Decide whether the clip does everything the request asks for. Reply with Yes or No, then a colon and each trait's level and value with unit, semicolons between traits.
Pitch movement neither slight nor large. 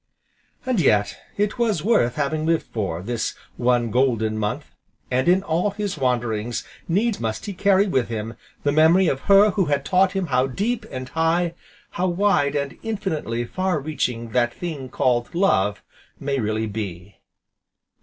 No: wide, 7.8 semitones